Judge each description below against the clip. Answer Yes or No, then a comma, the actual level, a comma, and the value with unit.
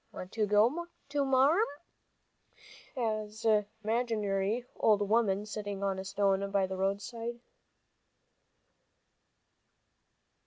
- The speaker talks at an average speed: No, slow, 85 wpm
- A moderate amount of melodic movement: Yes, average, 3.0 semitones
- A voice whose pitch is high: Yes, high, 210 Hz